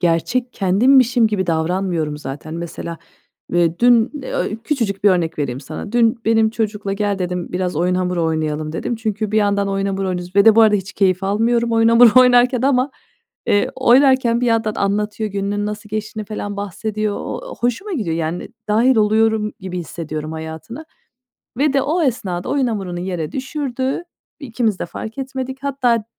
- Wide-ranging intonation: No, average, 4.8 semitones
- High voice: Yes, high, 210 Hz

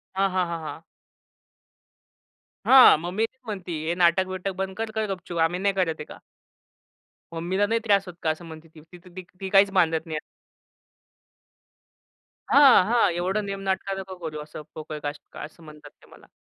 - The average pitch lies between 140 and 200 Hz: Yes, medium, 185 Hz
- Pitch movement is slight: No, average, 3.2 semitones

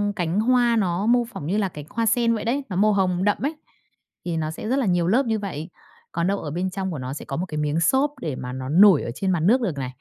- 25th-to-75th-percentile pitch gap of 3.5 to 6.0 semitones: Yes, wide, 5.6 semitones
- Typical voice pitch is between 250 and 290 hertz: No, high, 190 Hz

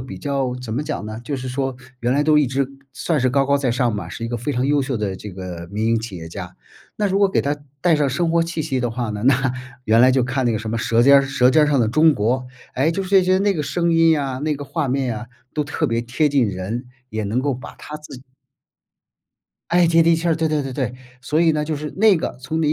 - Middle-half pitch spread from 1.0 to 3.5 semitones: No, average, 4.3 semitones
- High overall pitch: No, low, 135 Hz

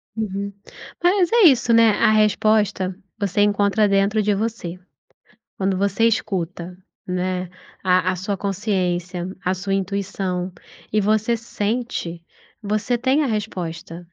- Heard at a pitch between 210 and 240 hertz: No, high, 200 Hz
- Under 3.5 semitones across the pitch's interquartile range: Yes, average, 2.8 semitones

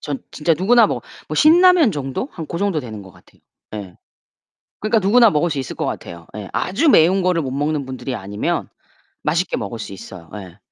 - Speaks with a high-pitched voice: No, medium, 150 Hz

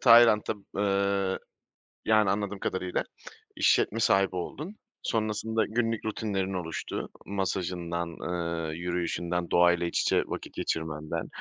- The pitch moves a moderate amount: Yes, average, 3.6 semitones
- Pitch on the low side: Yes, very low, 95 Hz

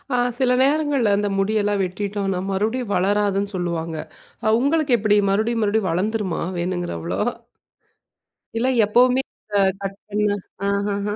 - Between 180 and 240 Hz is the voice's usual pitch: Yes, high, 205 Hz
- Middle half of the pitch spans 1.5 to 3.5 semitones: Yes, narrow, 2.6 semitones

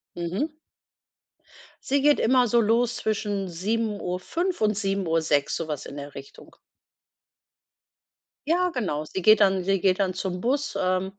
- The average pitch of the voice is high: Yes, high, 195 Hz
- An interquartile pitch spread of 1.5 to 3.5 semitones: No, average, 4.7 semitones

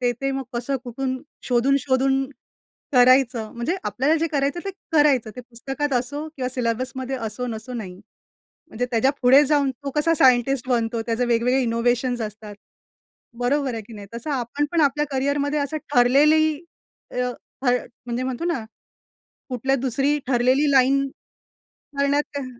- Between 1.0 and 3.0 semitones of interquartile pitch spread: Yes, narrow, 2.6 semitones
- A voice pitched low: No, very high, 260 Hz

